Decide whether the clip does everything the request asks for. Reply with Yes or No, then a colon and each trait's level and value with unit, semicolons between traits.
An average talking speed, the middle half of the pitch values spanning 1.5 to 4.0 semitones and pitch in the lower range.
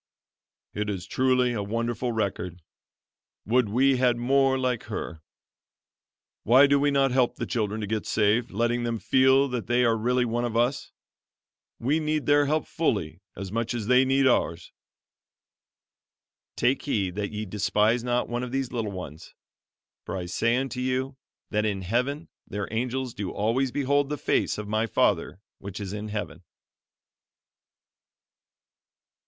Yes: average, 155 wpm; average, 3.7 semitones; low, 120 Hz